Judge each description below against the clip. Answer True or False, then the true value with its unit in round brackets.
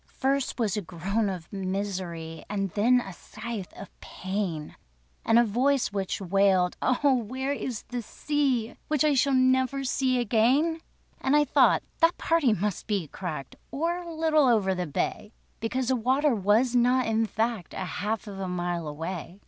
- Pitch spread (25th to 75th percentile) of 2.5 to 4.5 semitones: False (5.4 semitones)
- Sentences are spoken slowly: False (170 wpm)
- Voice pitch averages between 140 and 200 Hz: False (225 Hz)